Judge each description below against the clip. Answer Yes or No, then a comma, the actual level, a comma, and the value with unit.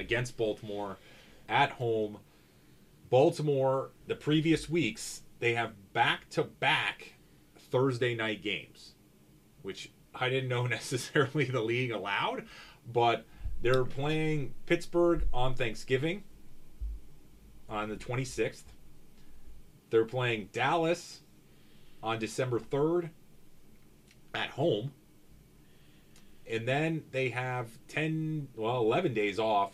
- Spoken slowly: Yes, slow, 100 wpm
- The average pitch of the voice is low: Yes, low, 130 Hz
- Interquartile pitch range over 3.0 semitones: Yes, average, 5.2 semitones